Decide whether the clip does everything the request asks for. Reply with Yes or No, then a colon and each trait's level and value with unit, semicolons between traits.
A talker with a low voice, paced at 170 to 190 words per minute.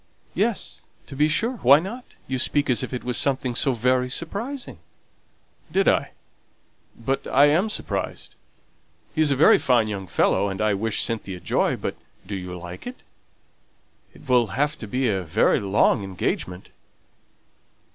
No: low, 125 Hz; average, 155 wpm